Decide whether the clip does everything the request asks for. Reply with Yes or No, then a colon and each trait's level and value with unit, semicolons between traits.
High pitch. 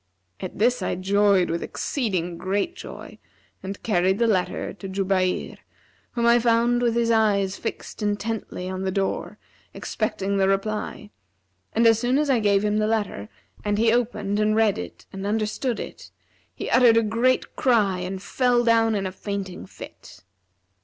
Yes: high, 210 Hz